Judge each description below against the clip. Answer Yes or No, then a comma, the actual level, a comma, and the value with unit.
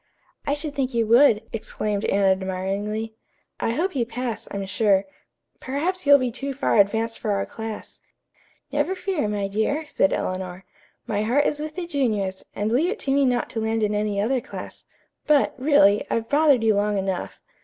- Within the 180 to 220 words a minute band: Yes, average, 185 wpm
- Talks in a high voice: Yes, high, 225 Hz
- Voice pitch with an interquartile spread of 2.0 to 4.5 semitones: No, wide, 5.6 semitones